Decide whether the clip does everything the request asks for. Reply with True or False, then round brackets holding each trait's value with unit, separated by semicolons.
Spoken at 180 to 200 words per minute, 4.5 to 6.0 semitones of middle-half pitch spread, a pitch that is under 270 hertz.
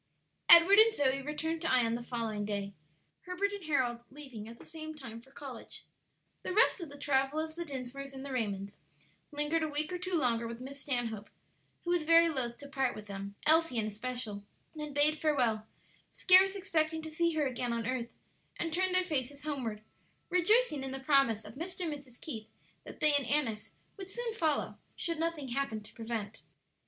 False (190 wpm; 5.3 semitones; 280 Hz)